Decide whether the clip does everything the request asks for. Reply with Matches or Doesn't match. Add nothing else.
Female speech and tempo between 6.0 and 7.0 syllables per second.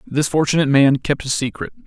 Doesn't match